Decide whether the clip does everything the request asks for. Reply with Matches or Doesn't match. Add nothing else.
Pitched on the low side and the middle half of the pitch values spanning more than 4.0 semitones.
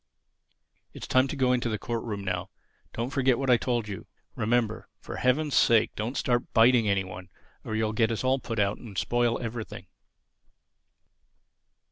Doesn't match